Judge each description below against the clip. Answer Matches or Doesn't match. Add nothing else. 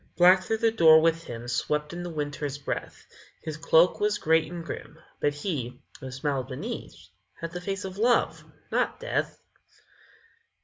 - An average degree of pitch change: Matches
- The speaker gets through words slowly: Doesn't match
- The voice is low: Doesn't match